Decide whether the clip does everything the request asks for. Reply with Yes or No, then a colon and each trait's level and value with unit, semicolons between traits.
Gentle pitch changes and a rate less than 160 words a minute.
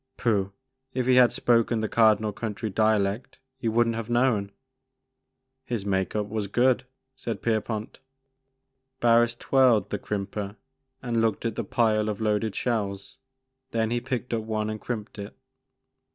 Yes: narrow, 2.2 semitones; average, 150 wpm